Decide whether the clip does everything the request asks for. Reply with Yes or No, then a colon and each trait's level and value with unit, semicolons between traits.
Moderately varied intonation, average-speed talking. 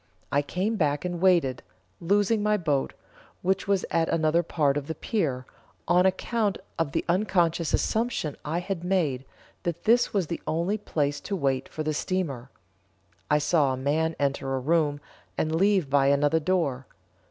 Yes: average, 4.6 semitones; average, 165 wpm